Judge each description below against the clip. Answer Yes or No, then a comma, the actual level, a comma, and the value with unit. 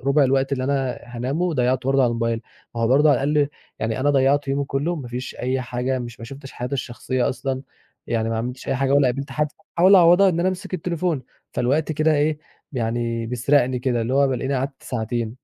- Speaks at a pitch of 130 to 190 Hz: Yes, low, 135 Hz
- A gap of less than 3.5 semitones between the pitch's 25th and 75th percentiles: Yes, average, 2.8 semitones